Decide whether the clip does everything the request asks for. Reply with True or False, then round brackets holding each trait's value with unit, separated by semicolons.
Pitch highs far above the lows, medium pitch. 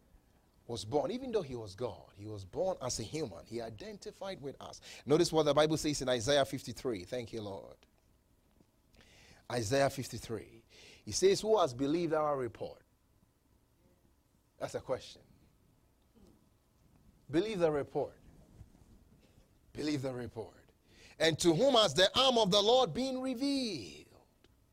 True (8.7 semitones; 150 Hz)